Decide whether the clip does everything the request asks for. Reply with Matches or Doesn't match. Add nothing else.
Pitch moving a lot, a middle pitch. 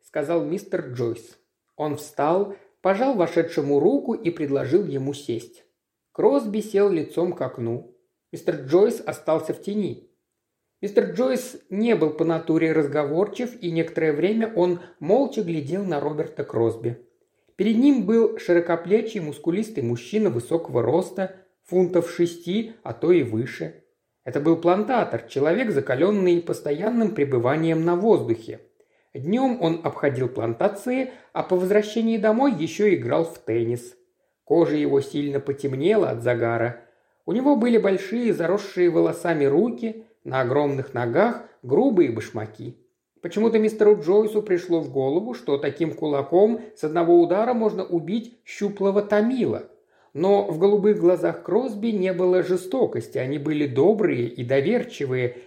Matches